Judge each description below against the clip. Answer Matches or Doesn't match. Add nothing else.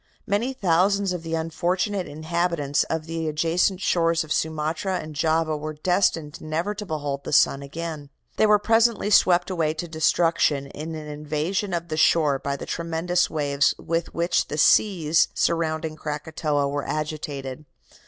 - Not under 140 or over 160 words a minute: Matches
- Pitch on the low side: Doesn't match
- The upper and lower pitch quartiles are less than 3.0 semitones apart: Matches